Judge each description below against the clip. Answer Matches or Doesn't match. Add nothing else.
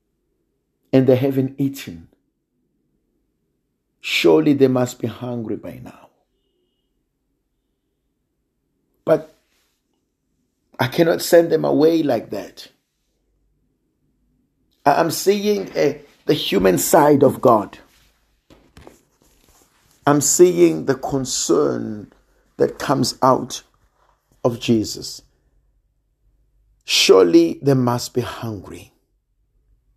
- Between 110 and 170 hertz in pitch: Matches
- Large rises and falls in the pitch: Doesn't match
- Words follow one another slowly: Matches